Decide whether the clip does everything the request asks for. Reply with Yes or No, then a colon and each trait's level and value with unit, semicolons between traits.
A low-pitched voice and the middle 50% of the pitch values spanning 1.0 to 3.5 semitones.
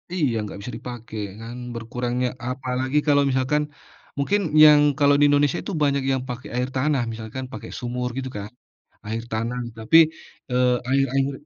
Yes: low, 130 Hz; narrow, 2.6 semitones